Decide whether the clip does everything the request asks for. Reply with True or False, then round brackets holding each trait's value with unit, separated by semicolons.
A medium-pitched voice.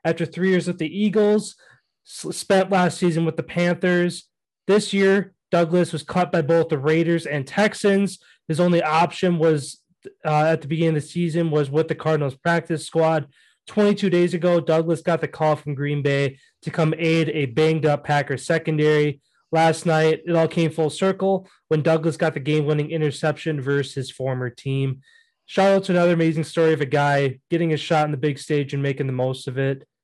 True (160 Hz)